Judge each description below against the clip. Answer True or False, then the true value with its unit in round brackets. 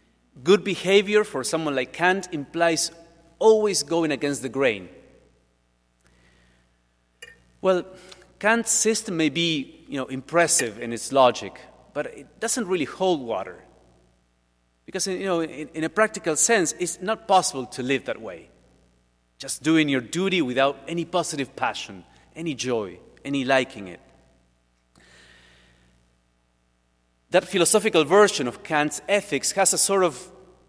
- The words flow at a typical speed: False (130 wpm)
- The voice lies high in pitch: False (145 Hz)